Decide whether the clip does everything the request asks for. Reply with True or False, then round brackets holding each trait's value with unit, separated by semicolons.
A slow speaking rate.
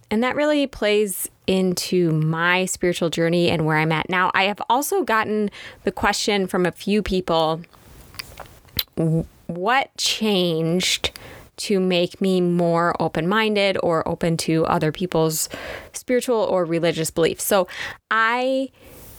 True (130 wpm)